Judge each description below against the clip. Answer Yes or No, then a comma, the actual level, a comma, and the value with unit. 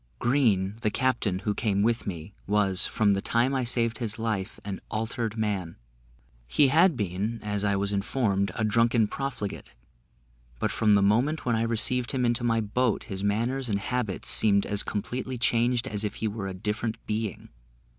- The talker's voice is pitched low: Yes, low, 110 Hz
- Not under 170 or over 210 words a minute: Yes, average, 180 wpm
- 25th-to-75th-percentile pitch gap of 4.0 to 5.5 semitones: No, average, 3.0 semitones